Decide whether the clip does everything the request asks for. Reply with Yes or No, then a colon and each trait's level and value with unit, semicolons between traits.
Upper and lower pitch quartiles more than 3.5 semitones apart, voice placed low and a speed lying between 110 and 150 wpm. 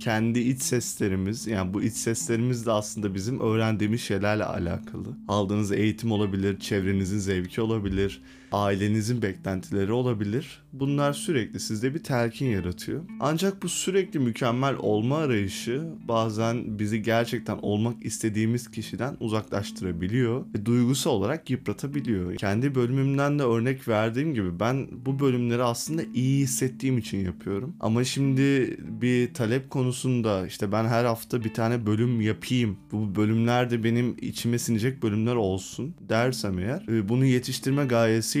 No: average, 3.2 semitones; low, 115 Hz; average, 135 wpm